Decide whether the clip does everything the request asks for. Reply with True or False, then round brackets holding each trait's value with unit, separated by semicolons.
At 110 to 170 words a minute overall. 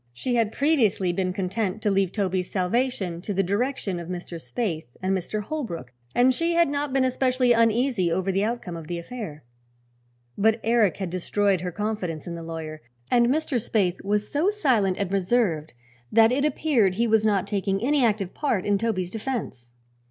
False (180 wpm)